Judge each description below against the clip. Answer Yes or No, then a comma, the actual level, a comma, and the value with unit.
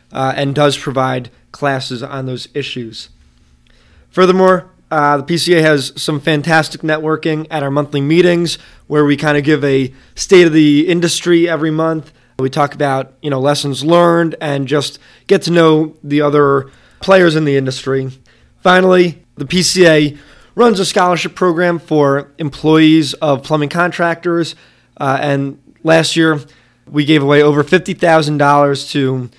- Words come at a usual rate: Yes, average, 150 wpm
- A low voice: No, medium, 150 Hz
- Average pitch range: Yes, average, 3.2 semitones